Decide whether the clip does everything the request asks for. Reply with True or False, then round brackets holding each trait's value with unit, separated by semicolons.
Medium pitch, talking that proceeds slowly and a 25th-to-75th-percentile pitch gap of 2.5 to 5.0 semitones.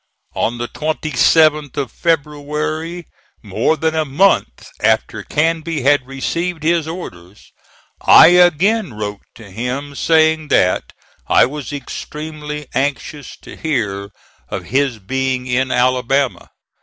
True (145 Hz; 120 wpm; 3.8 semitones)